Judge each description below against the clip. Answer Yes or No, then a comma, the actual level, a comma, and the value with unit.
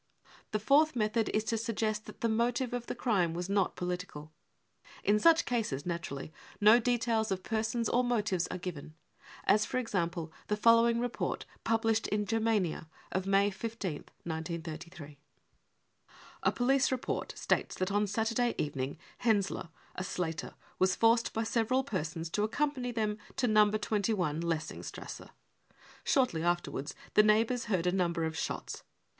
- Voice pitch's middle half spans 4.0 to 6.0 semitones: Yes, average, 4.8 semitones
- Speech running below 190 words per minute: Yes, average, 150 wpm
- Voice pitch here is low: No, high, 210 Hz